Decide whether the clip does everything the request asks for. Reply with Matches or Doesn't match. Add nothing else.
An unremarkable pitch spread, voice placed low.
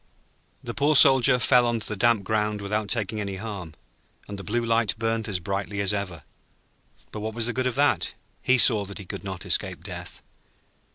Matches